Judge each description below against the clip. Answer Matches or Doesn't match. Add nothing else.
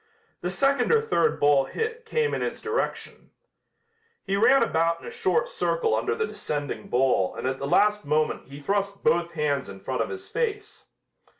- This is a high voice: Matches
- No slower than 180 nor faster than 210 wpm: Matches